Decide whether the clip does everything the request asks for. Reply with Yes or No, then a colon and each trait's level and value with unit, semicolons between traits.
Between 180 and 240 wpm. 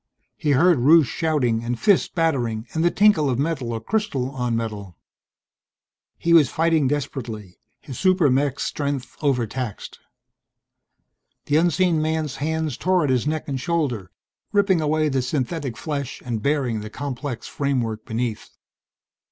No: average, 145 wpm